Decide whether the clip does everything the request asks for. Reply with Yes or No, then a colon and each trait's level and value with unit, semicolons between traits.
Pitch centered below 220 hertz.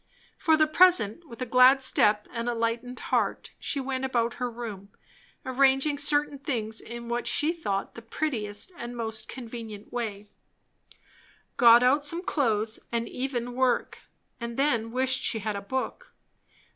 No: high, 245 Hz